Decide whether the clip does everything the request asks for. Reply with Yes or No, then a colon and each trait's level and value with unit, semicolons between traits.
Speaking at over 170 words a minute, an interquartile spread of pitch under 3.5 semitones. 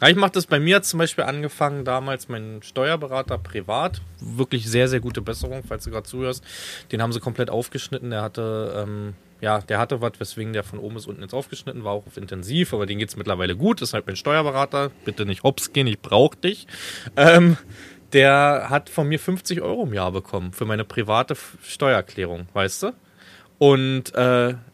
No: fast, 190 wpm; average, 4.9 semitones